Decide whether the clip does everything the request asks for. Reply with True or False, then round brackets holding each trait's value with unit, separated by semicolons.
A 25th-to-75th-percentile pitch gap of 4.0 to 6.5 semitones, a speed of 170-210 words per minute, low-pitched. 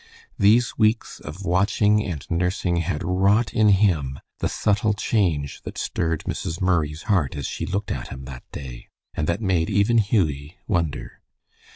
False (5.4 semitones; 160 wpm; 90 Hz)